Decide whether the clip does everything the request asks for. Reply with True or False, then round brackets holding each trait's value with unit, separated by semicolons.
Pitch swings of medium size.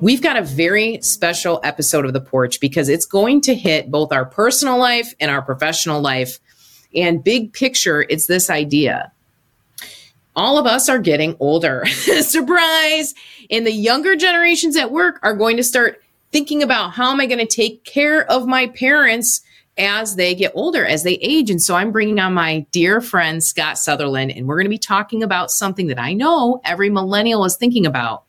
False (7.8 semitones)